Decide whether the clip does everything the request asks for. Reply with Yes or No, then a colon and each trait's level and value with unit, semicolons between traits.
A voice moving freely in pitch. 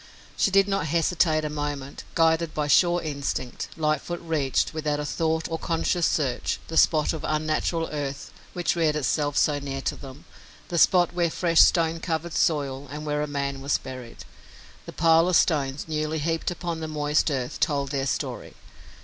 No: narrow, 2.4 semitones